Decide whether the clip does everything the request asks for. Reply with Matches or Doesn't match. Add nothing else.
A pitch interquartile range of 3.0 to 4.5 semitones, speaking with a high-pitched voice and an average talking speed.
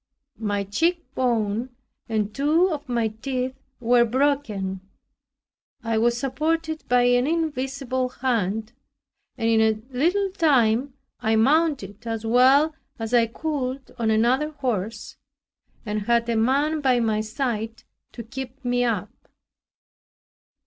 Doesn't match